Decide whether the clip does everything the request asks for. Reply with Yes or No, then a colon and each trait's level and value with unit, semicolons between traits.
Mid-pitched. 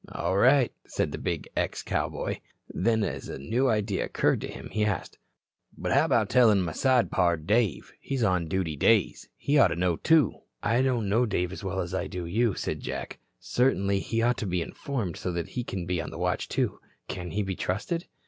No: low, 100 Hz